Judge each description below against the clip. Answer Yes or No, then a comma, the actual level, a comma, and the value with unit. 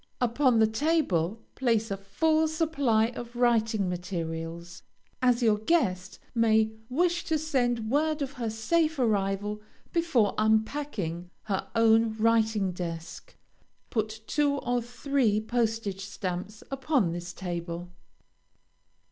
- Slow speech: Yes, slow, 115 wpm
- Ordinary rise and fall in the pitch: Yes, average, 5.0 semitones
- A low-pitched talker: No, high, 220 Hz